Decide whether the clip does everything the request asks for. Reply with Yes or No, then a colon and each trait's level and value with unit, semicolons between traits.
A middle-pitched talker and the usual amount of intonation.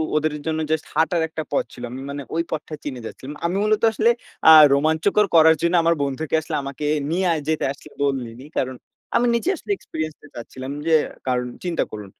Yes: medium, 155 Hz; average, 3.5 semitones